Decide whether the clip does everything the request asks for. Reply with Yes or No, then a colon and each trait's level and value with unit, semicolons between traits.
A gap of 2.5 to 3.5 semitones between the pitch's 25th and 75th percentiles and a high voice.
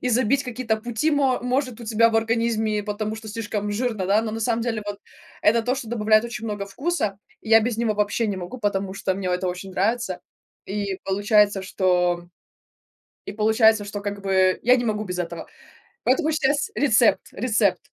Yes: average, 2.8 semitones; high, 215 Hz